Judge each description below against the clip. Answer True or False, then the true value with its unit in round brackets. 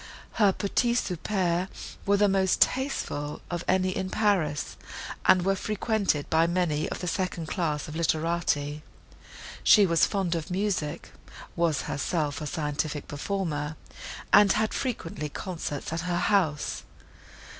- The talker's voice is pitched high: False (175 Hz)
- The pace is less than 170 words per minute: True (135 wpm)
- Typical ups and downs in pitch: True (4.2 semitones)